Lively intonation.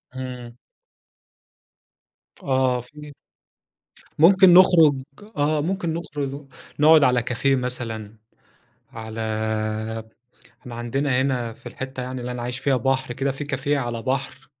No: average, 2.8 semitones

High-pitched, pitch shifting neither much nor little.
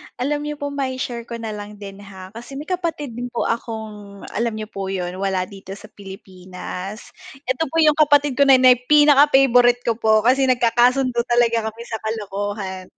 Yes: high, 230 Hz; average, 4.3 semitones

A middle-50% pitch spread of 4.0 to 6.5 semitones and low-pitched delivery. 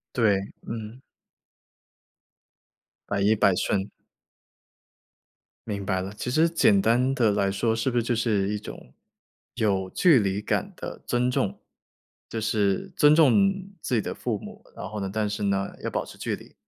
No: average, 3.5 semitones; low, 105 Hz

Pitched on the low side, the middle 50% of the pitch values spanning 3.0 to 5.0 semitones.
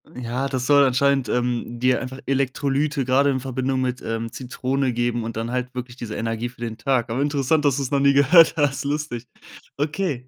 No: low, 130 Hz; narrow, 2.4 semitones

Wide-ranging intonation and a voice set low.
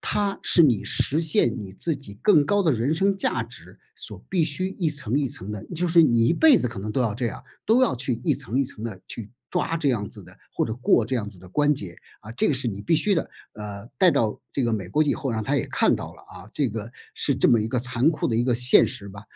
Yes: wide, 6.0 semitones; low, 125 Hz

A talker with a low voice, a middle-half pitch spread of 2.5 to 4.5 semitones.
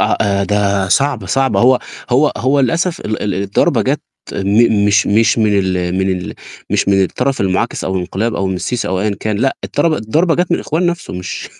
No: low, 105 Hz; wide, 5.6 semitones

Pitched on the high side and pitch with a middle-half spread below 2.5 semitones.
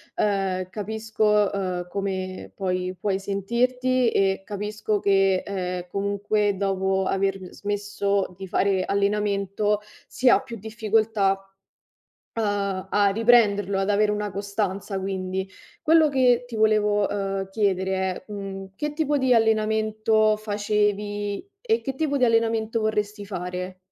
Yes: high, 205 Hz; narrow, 2.0 semitones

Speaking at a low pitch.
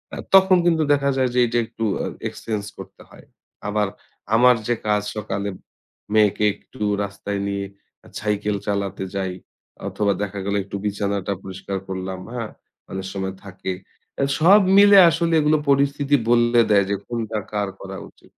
Yes: low, 105 Hz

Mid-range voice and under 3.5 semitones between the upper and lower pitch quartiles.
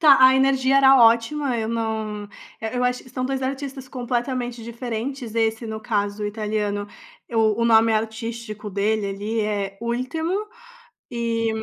No: high, 230 Hz; average, 2.8 semitones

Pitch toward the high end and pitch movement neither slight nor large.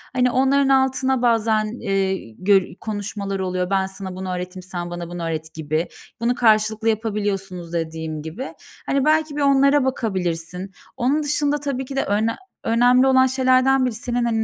No: high, 220 Hz; wide, 5.9 semitones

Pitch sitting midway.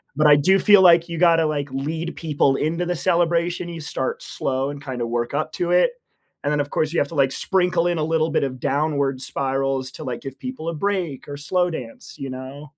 Yes: medium, 150 Hz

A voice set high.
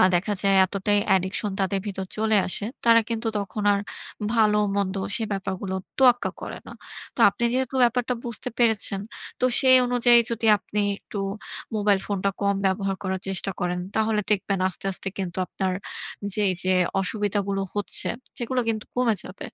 Yes: high, 205 Hz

